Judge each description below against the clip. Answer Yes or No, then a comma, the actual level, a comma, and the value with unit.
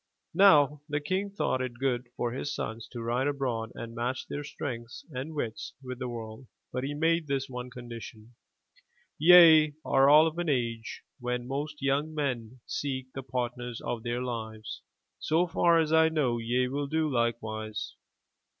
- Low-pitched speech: Yes, low, 130 Hz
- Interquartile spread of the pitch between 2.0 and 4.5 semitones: Yes, average, 3.9 semitones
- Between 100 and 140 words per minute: No, average, 170 wpm